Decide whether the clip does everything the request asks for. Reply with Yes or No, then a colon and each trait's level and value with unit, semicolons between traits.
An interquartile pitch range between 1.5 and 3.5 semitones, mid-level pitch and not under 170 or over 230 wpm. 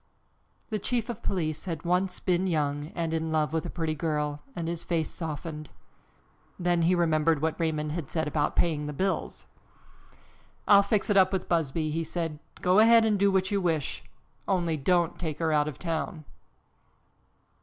Yes: average, 2.9 semitones; medium, 165 Hz; average, 175 wpm